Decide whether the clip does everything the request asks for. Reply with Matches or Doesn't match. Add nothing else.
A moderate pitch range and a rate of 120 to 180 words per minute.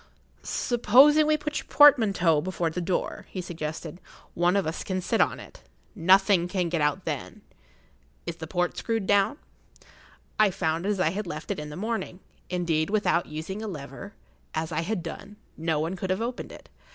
Doesn't match